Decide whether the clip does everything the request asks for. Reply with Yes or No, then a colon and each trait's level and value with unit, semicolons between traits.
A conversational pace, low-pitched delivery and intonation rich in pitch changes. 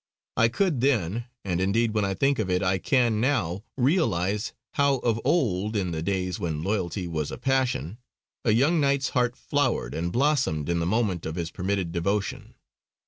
Yes: average, 180 wpm; low, 105 Hz; wide, 6.2 semitones